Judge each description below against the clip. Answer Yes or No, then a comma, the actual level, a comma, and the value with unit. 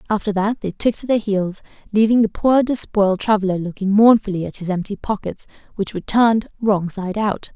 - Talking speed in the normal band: Yes, average, 190 wpm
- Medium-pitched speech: No, high, 205 Hz